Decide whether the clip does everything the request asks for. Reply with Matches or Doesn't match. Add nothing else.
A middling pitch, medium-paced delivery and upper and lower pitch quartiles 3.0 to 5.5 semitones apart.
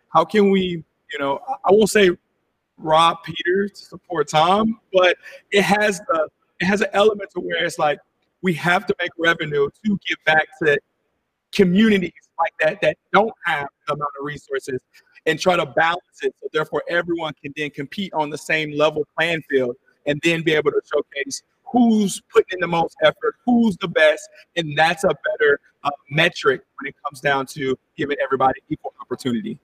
Matches